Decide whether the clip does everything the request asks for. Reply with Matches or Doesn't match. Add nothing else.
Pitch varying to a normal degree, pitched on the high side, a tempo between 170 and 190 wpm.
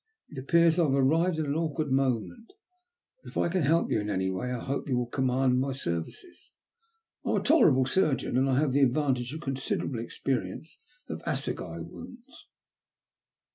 Doesn't match